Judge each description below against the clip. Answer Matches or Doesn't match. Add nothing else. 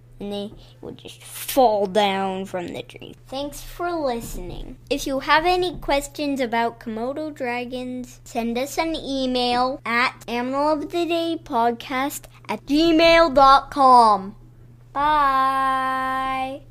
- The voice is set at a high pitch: Matches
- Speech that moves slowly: Matches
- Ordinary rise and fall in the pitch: Matches